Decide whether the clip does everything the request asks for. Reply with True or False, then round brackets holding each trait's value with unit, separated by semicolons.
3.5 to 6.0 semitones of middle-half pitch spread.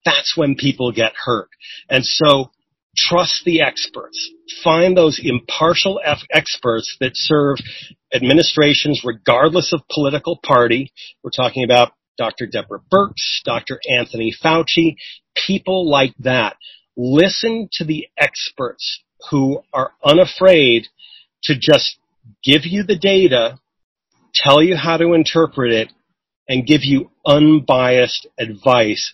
True (4.9 semitones)